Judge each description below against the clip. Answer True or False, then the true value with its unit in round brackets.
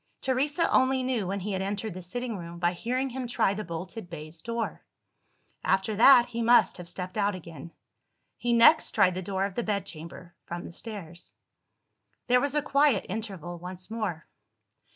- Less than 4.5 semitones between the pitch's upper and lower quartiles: False (5.2 semitones)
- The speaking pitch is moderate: False (200 Hz)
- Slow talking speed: False (175 wpm)